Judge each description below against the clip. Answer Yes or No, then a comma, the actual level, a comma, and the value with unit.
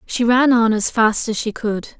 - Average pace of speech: No, fast, 240 wpm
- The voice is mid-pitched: No, high, 225 Hz